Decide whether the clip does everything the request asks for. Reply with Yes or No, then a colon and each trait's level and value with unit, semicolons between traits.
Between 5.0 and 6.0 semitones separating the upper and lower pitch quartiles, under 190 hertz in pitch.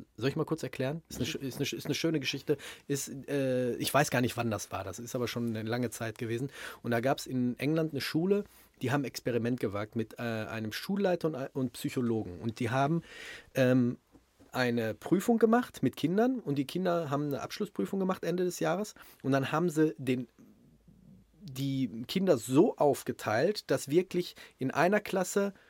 Yes: wide, 5.4 semitones; low, 135 Hz